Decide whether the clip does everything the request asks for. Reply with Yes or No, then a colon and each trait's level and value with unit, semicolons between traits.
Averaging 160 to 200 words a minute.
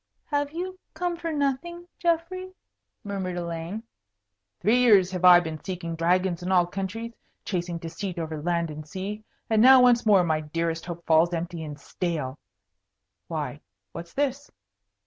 No: average, 150 wpm